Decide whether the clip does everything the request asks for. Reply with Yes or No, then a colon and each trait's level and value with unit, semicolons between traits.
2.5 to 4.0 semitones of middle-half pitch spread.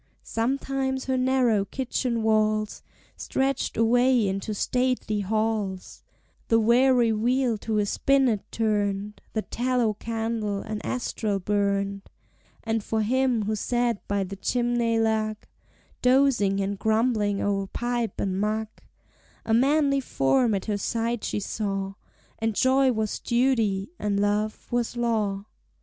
Yes: average, 3.1 semitones